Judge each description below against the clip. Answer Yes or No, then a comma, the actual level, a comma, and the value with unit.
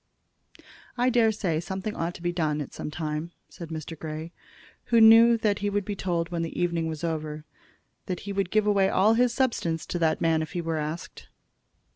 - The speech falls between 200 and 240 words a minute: Yes, fast, 205 wpm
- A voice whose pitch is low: No, medium, 175 Hz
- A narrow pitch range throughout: No, average, 4.2 semitones